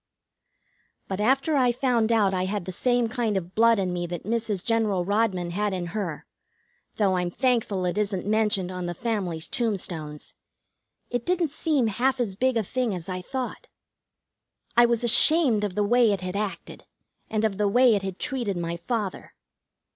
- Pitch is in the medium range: No, high, 210 Hz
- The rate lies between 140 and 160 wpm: No, average, 180 wpm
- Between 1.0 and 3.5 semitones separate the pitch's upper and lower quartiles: No, average, 4.4 semitones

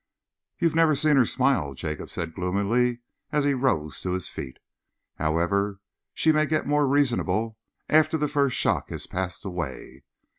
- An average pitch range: No, wide, 8.5 semitones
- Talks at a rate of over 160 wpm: No, average, 155 wpm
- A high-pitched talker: No, low, 120 Hz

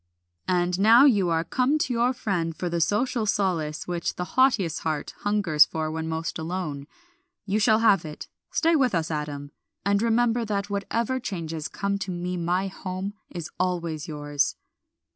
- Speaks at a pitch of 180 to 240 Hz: Yes, medium, 185 Hz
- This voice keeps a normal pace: Yes, average, 165 wpm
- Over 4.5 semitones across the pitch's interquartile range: Yes, average, 4.9 semitones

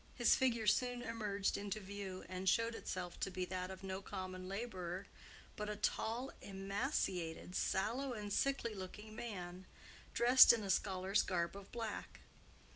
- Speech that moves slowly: No, average, 150 wpm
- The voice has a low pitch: No, high, 200 Hz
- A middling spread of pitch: Yes, average, 3.6 semitones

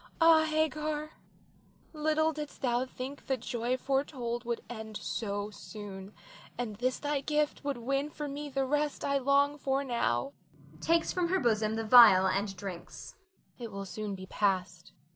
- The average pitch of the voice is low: No, very high, 255 Hz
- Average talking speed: Yes, average, 160 wpm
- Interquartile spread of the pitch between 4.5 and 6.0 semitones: Yes, wide, 5.6 semitones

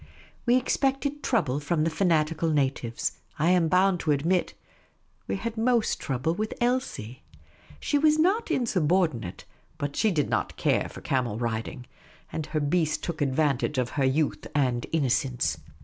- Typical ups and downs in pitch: No, wide, 6.9 semitones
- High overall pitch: No, medium, 155 Hz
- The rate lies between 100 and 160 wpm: Yes, average, 150 wpm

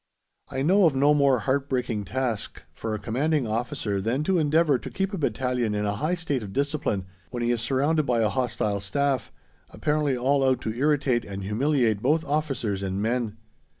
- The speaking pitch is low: Yes, low, 130 Hz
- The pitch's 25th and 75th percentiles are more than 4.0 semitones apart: Yes, average, 4.8 semitones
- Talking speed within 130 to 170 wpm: No, average, 190 wpm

